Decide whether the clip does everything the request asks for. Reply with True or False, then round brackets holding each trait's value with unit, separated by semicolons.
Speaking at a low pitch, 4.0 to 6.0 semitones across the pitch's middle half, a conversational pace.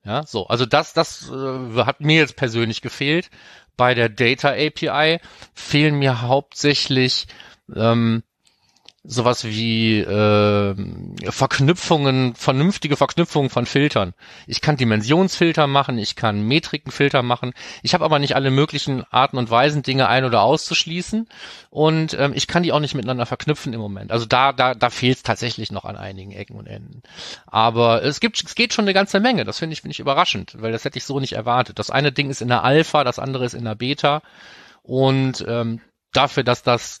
True (130 Hz; 4.3 semitones; 180 wpm)